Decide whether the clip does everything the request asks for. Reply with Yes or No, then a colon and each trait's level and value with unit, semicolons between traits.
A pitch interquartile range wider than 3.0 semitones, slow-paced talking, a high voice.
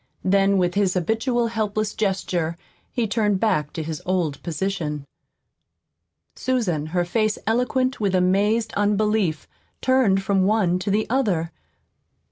Yes: average, 3.6 semitones; slow, 125 wpm; high, 200 Hz